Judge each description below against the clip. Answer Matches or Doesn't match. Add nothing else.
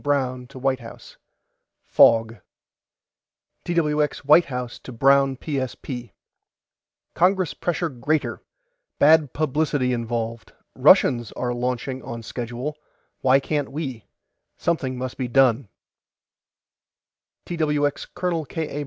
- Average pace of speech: Doesn't match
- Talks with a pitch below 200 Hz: Matches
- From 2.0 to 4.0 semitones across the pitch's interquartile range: Matches